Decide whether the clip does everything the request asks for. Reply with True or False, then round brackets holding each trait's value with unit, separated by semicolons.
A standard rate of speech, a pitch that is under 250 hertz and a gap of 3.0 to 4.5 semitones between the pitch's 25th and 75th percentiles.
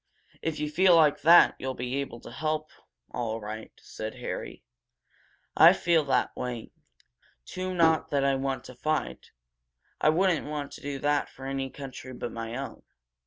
True (165 wpm; 140 Hz; 3.6 semitones)